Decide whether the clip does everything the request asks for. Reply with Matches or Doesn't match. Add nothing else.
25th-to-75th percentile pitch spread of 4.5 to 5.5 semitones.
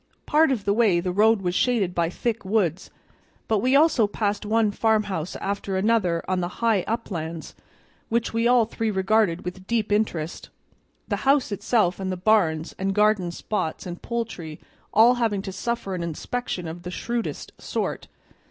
Doesn't match